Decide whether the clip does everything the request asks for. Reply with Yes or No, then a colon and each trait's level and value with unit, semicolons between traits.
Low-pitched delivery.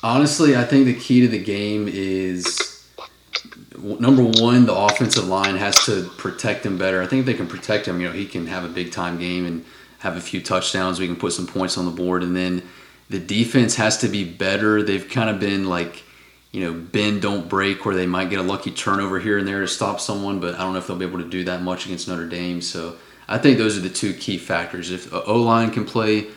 Yes: very low, 95 Hz